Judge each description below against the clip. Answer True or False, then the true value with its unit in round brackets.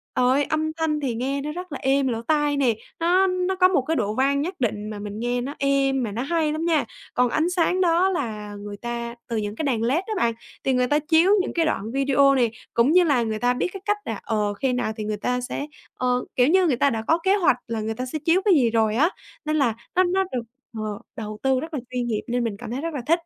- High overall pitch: True (265 Hz)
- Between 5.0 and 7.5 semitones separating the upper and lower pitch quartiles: True (5.5 semitones)